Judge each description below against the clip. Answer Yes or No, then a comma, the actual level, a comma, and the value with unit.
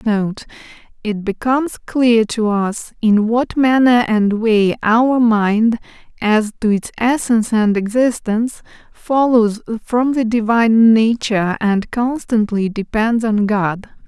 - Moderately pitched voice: No, high, 225 Hz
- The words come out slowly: Yes, slow, 125 wpm